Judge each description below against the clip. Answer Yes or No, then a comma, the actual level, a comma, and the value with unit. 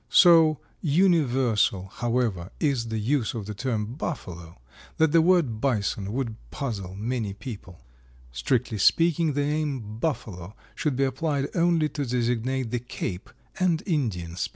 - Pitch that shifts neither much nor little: No, wide, 6.0 semitones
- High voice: No, low, 125 Hz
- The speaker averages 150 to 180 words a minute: No, average, 140 wpm